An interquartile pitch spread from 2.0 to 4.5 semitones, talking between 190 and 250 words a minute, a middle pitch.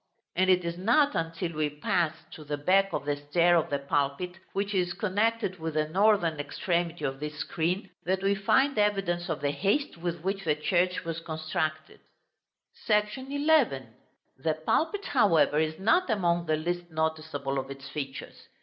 No: average, 4.1 semitones; average, 170 wpm; medium, 170 Hz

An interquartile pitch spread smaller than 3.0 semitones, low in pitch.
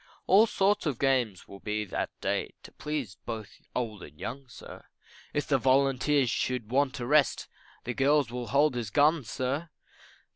No: average, 4.1 semitones; low, 130 Hz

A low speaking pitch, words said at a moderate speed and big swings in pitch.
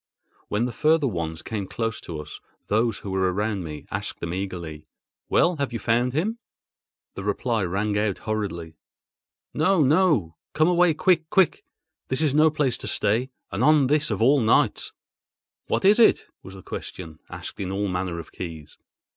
Yes: low, 110 Hz; average, 170 wpm; wide, 8.3 semitones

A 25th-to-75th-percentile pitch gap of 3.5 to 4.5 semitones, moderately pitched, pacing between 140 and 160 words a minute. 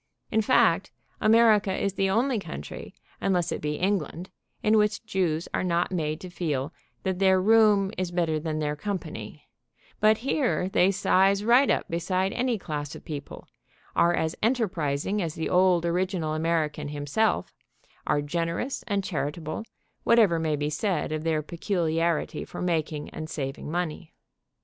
Yes: average, 4.2 semitones; medium, 175 Hz; average, 155 wpm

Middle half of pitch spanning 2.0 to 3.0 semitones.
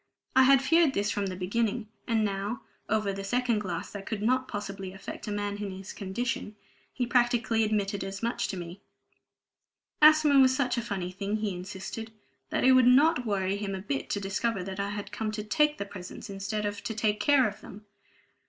No: average, 3.5 semitones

